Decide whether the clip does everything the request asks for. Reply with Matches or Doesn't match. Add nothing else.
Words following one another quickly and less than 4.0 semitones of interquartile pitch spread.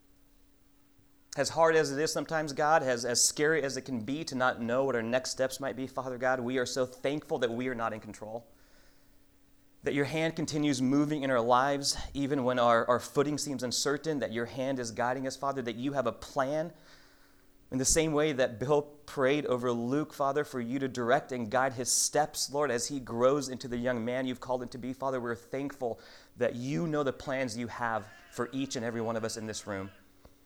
Matches